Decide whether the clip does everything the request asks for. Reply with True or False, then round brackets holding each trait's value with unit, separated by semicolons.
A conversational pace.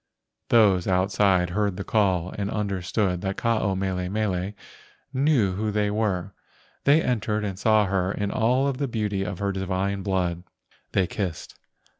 True (160 wpm)